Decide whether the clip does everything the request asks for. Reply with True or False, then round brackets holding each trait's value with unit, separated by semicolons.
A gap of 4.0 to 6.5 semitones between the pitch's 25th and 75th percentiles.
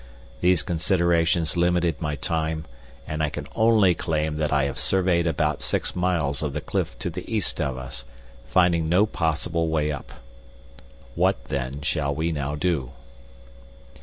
False (3.0 semitones)